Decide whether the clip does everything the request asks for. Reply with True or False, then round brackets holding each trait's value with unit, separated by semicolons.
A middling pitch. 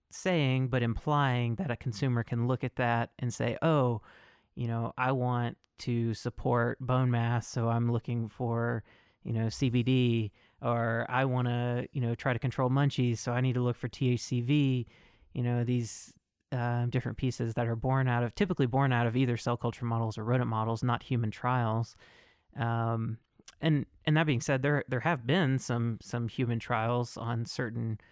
False (120 Hz)